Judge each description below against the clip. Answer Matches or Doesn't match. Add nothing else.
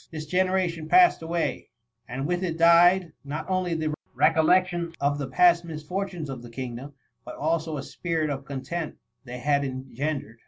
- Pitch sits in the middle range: Matches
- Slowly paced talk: Doesn't match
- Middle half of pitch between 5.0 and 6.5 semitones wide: Doesn't match